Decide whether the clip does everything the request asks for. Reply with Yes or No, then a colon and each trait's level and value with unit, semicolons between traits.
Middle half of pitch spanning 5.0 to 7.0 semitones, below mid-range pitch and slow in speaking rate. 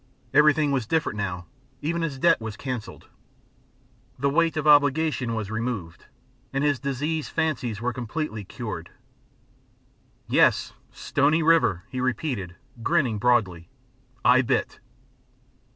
Yes: wide, 5.6 semitones; low, 130 Hz; slow, 120 wpm